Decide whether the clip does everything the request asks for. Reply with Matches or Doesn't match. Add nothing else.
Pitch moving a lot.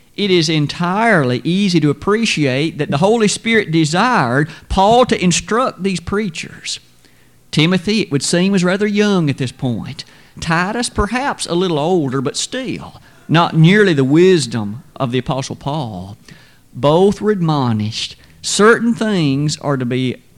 Matches